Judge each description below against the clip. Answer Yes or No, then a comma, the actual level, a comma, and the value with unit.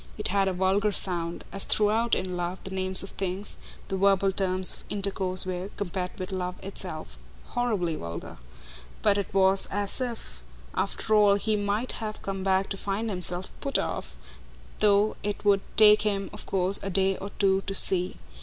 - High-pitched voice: Yes, high, 195 Hz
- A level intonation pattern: Yes, narrow, 1.6 semitones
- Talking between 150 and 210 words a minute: Yes, average, 180 wpm